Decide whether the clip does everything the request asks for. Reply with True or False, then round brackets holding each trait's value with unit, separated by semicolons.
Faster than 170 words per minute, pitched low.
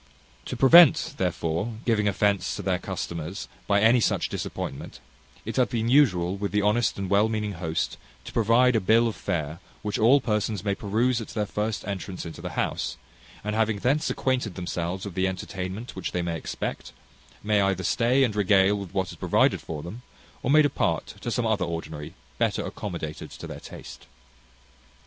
True (180 wpm; 105 Hz)